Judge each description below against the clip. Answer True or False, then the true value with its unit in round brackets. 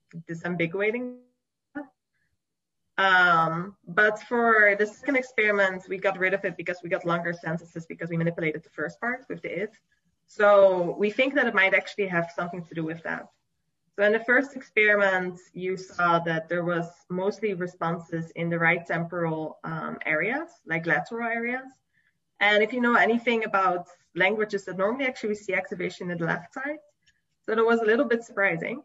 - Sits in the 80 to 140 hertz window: False (195 Hz)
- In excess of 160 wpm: True (175 wpm)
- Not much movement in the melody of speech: False (4.7 semitones)